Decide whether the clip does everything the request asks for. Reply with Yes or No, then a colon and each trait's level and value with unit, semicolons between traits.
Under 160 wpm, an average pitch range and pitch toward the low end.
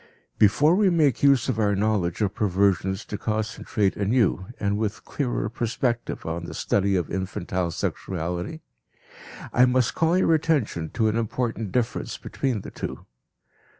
Yes: average, 150 wpm; average, 4.8 semitones; low, 110 Hz